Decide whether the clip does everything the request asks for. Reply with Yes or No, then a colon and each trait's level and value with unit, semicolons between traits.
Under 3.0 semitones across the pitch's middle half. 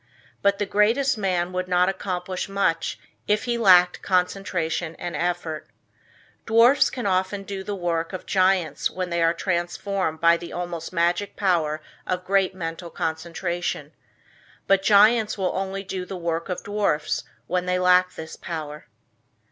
Yes: narrow, 2.4 semitones